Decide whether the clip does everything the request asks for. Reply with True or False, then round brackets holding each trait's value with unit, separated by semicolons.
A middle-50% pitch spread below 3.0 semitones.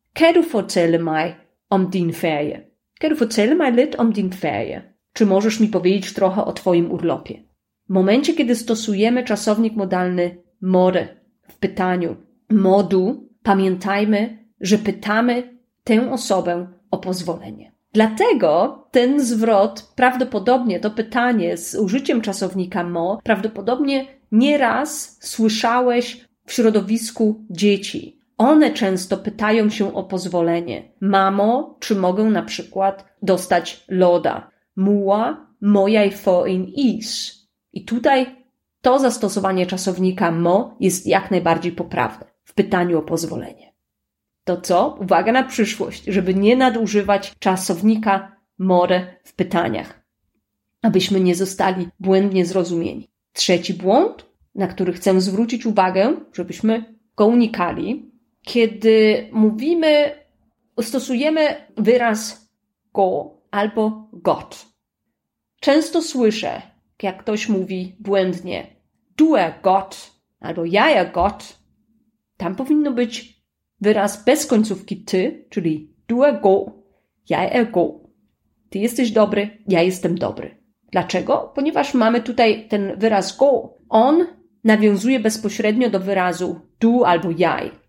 False (4.2 semitones)